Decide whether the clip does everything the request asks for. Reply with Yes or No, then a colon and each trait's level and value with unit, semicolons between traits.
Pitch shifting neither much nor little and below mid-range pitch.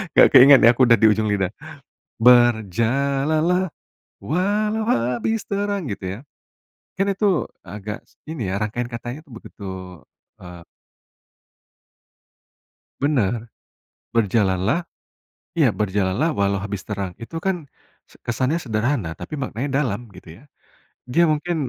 No: wide, 7.0 semitones; low, 120 Hz